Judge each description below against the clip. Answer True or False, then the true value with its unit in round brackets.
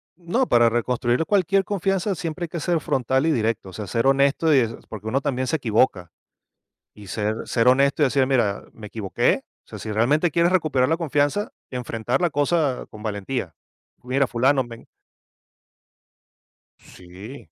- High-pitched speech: False (130 Hz)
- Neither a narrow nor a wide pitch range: False (5.7 semitones)